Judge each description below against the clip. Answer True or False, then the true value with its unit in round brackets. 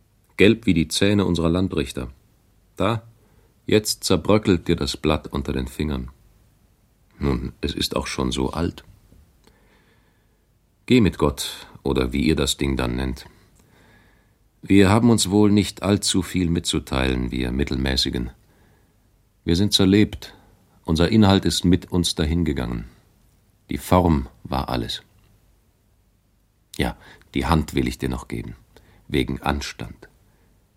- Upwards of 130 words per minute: False (125 wpm)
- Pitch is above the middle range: False (90 Hz)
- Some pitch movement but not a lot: False (6.2 semitones)